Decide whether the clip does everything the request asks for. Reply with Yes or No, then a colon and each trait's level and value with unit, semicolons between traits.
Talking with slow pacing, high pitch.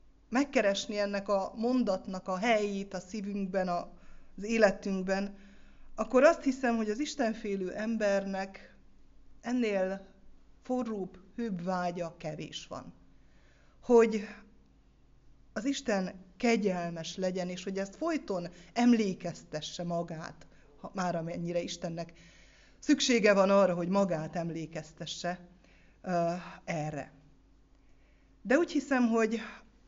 Yes: slow, 100 wpm; high, 195 Hz